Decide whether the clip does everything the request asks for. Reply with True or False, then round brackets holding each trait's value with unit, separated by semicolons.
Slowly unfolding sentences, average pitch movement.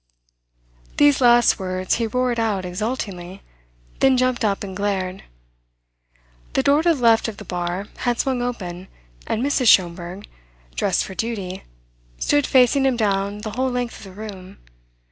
False (155 wpm; 4.7 semitones)